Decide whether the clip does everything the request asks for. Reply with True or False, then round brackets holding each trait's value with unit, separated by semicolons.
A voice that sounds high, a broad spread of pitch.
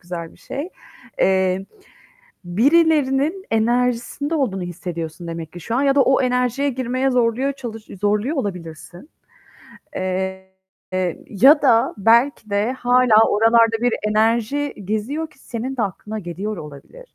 True (230 Hz; 6.0 semitones)